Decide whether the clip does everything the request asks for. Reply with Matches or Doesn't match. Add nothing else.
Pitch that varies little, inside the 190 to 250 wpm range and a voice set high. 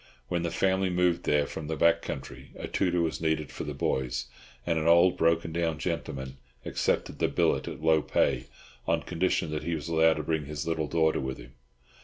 Doesn't match